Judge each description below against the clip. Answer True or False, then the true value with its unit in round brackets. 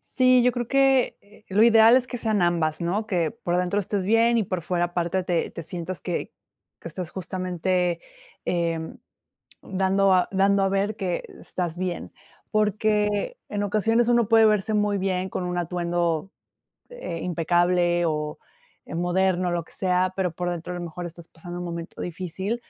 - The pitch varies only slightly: False (3.1 semitones)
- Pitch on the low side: False (185 Hz)